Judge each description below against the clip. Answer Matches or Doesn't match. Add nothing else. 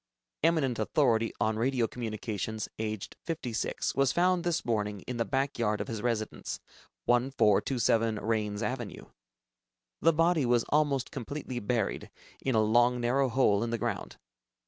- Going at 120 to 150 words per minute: Matches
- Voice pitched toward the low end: Matches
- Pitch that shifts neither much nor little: Matches